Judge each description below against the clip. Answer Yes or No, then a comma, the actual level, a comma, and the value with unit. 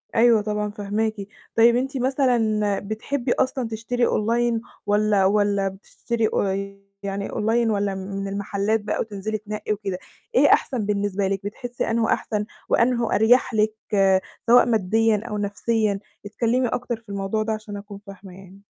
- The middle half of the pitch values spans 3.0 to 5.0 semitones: No, narrow, 2.4 semitones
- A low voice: No, high, 215 Hz